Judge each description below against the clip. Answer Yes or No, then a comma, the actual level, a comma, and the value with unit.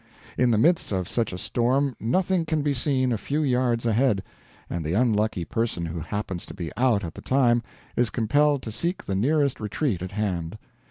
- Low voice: Yes, low, 115 Hz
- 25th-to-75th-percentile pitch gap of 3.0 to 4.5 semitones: No, wide, 5.5 semitones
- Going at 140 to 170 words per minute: No, average, 200 wpm